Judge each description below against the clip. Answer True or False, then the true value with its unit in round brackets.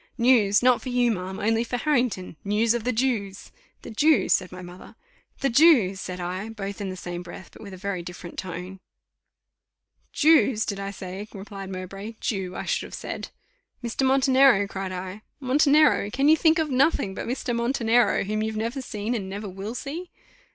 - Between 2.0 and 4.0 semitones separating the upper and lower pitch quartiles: False (4.7 semitones)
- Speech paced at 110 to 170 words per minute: False (185 wpm)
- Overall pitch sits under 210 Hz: False (215 Hz)